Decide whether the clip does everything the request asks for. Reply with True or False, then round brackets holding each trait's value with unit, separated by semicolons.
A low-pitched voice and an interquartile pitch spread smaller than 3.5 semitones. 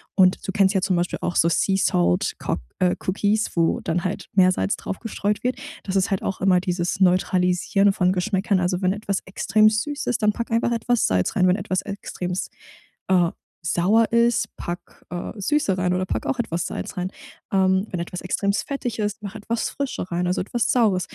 False (190 Hz; 2.9 semitones)